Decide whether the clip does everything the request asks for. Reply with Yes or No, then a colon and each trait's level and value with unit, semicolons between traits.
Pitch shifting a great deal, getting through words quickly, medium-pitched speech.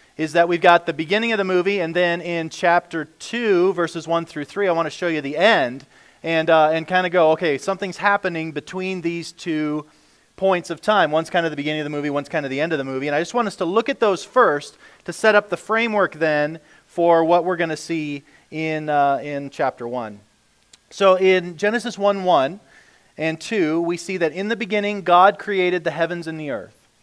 No: average, 3.3 semitones; fast, 230 wpm; medium, 170 Hz